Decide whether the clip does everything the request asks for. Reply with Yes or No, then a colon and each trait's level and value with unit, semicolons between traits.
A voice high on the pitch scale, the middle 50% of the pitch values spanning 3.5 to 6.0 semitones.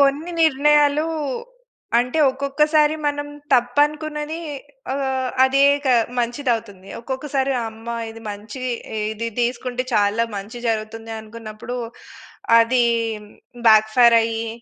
Yes: very high, 250 Hz; average, 4.2 semitones